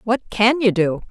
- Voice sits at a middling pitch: No, high, 215 Hz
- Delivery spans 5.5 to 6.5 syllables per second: No, 4.3 syllables/s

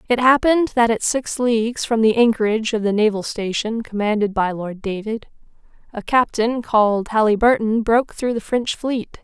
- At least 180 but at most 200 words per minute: No, average, 170 wpm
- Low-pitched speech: No, high, 225 Hz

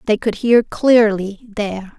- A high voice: Yes, high, 215 Hz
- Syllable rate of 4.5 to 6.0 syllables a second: No, 4.0 syllables/s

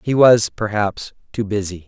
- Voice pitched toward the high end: No, low, 105 Hz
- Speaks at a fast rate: No, average, 160 wpm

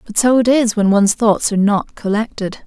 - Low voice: No, high, 215 Hz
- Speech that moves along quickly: Yes, fast, 225 wpm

